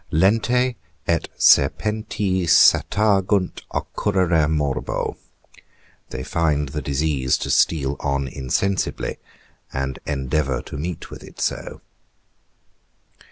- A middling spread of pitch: No, wide, 5.7 semitones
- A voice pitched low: Yes, very low, 80 Hz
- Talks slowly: Yes, slow, 95 wpm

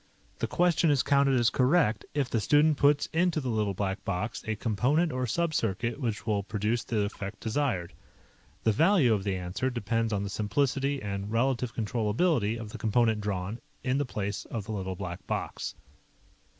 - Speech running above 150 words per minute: Yes, average, 175 wpm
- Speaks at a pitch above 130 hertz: No, low, 115 Hz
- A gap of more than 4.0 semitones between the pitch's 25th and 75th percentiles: Yes, average, 5.0 semitones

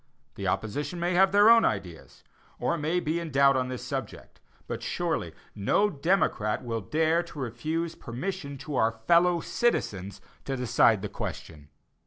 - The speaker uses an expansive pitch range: Yes, wide, 7.3 semitones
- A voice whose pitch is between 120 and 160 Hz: Yes, medium, 140 Hz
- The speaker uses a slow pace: No, average, 165 wpm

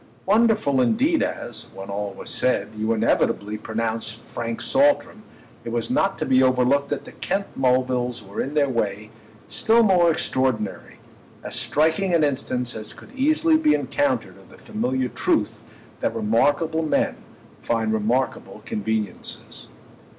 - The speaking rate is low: No, average, 145 wpm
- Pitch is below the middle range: Yes, low, 130 Hz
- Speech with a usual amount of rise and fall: No, wide, 8.1 semitones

